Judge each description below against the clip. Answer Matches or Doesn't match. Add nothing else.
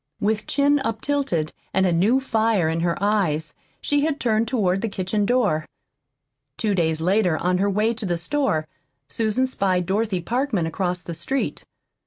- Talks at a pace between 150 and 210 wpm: Matches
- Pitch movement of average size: Matches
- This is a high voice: Matches